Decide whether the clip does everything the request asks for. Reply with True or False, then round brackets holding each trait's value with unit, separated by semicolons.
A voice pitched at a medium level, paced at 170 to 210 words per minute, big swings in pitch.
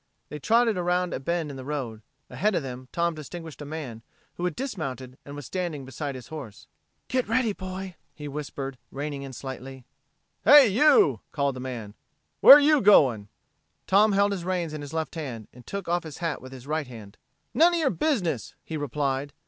True (150 Hz; 195 wpm; 5.8 semitones)